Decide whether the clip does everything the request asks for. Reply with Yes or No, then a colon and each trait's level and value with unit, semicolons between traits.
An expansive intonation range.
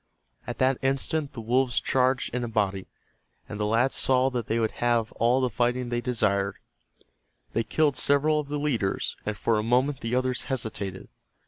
No: average, 3.0 semitones